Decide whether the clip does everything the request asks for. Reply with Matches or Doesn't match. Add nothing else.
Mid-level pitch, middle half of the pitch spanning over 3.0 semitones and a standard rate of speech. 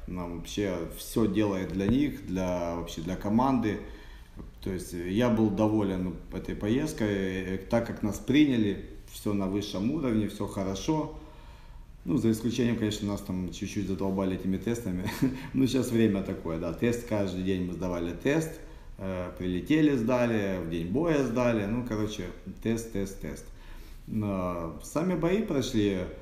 Doesn't match